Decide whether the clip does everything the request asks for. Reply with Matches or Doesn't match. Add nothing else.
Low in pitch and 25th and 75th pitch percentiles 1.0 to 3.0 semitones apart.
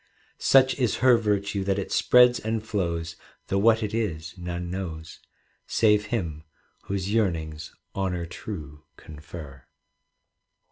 Doesn't match